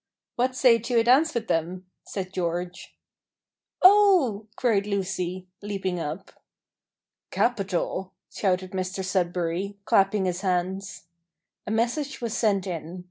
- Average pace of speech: No, slow, 120 wpm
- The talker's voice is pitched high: Yes, high, 195 Hz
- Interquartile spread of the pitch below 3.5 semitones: No, average, 3.9 semitones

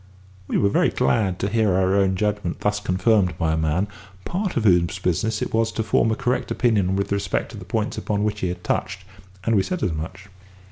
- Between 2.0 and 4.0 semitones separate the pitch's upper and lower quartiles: Yes, average, 3.1 semitones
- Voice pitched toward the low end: Yes, low, 100 Hz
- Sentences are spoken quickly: Yes, fast, 225 wpm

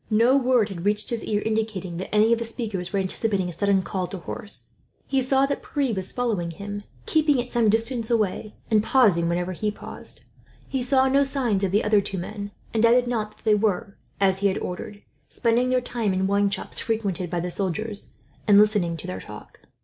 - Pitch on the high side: Yes, high, 210 Hz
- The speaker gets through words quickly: Yes, fast, 210 wpm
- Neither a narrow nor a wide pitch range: Yes, average, 3.6 semitones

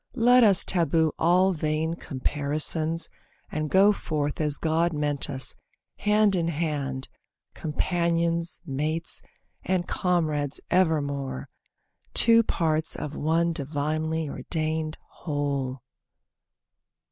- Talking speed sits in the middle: No, slow, 100 wpm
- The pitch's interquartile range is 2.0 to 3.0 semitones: Yes, narrow, 2.5 semitones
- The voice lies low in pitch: No, medium, 160 Hz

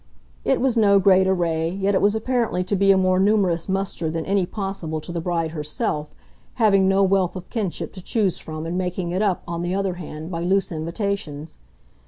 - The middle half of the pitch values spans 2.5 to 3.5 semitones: Yes, average, 2.8 semitones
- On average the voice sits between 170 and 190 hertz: Yes, medium, 185 Hz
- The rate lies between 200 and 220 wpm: Yes, fast, 205 wpm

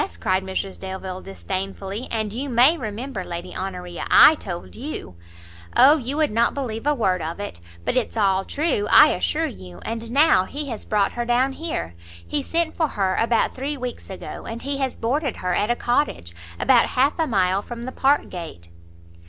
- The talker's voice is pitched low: No, high, 230 Hz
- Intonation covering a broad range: Yes, wide, 6.4 semitones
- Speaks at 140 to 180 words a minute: No, average, 195 wpm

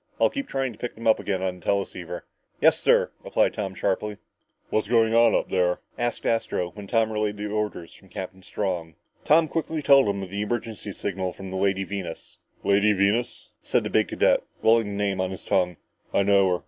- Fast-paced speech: Yes, fast, 215 wpm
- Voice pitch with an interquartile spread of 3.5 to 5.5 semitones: No, average, 2.9 semitones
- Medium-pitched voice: No, low, 100 Hz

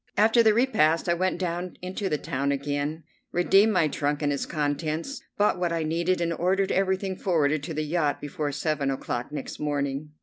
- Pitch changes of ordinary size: Yes, average, 4.0 semitones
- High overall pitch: No, medium, 160 Hz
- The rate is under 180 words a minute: No, average, 190 wpm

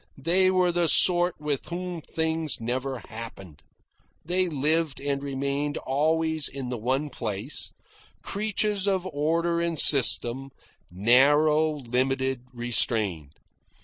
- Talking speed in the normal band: No, slow, 115 wpm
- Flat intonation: No, average, 4.7 semitones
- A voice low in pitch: No, medium, 145 Hz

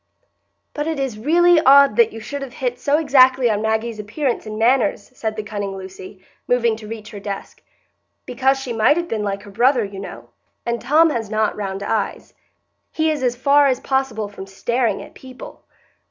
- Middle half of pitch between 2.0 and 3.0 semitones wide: No, average, 4.3 semitones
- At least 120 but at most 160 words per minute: No, average, 200 wpm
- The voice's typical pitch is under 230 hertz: No, high, 235 Hz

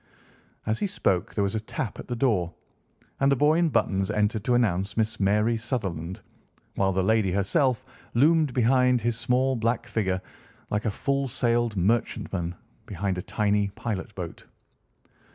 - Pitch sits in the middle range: No, low, 110 Hz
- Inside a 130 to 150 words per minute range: No, average, 165 wpm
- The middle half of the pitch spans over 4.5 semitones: No, average, 4.2 semitones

